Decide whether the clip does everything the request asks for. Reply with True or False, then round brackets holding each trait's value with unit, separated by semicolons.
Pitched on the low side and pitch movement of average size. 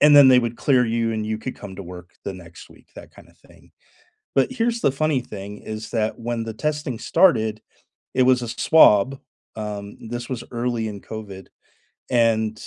True (115 Hz; 3.3 semitones)